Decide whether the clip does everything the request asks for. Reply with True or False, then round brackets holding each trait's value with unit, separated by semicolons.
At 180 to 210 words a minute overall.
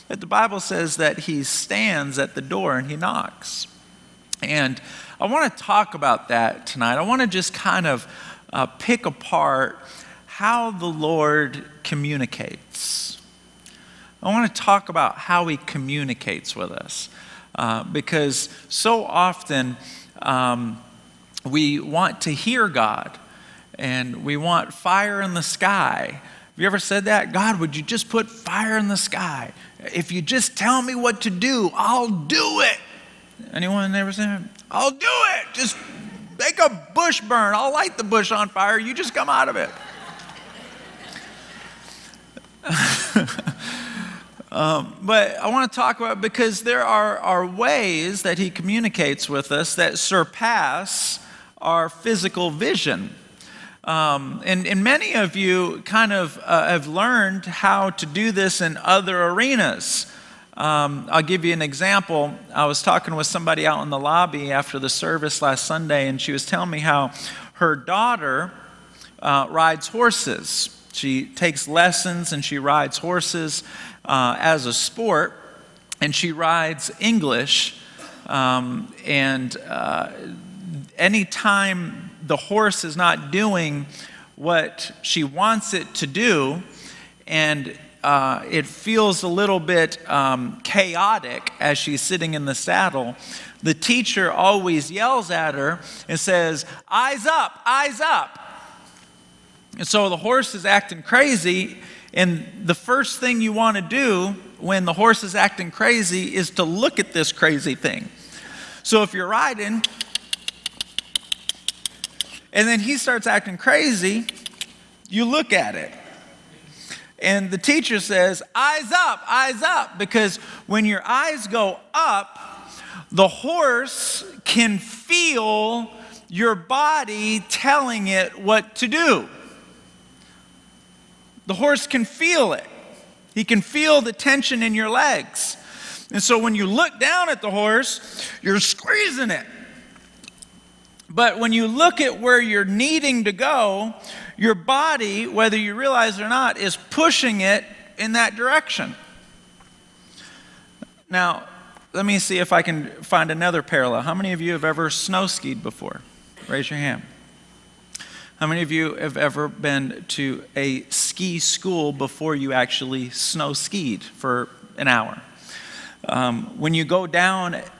False (140 wpm)